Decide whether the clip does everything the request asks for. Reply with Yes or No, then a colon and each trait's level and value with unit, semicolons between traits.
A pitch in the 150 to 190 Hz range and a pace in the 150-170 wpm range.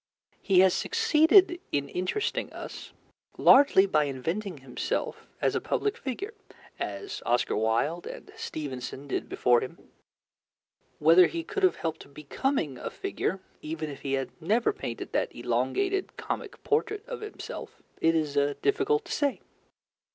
No: medium, 185 Hz; average, 140 wpm